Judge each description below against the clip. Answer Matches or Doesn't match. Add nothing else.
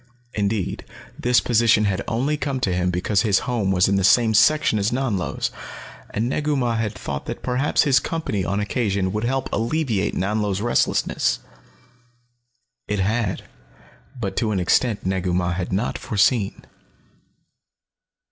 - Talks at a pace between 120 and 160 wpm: Matches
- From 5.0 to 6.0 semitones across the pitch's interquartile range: Doesn't match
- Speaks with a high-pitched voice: Doesn't match